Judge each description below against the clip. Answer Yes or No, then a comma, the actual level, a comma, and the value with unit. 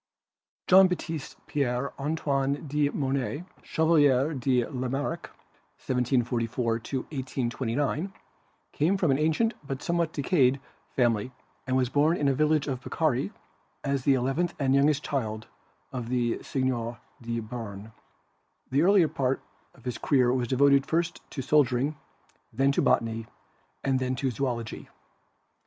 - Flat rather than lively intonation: No, average, 3.1 semitones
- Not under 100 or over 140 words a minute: Yes, slow, 135 wpm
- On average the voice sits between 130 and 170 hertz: Yes, low, 135 Hz